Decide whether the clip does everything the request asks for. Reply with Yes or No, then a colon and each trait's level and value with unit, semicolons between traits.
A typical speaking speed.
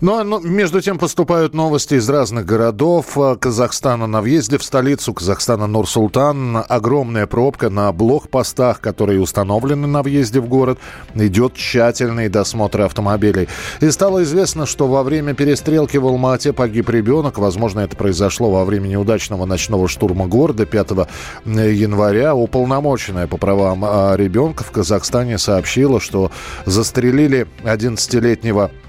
Yes: average, 125 wpm